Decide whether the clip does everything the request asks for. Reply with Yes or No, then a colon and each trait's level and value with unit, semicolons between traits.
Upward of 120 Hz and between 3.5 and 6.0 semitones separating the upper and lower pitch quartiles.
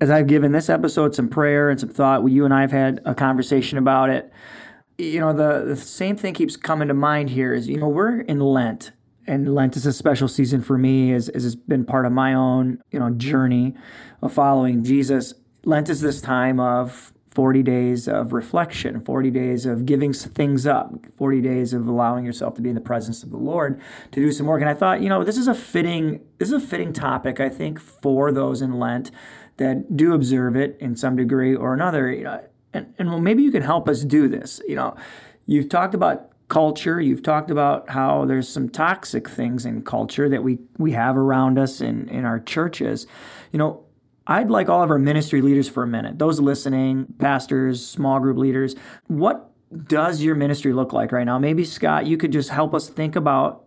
No: low, 135 Hz; average, 2.7 semitones